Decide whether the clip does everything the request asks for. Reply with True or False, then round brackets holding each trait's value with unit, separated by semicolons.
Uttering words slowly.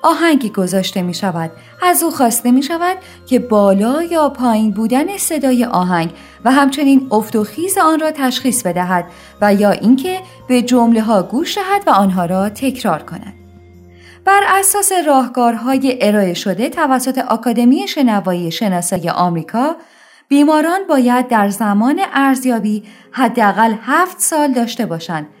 False (140 wpm)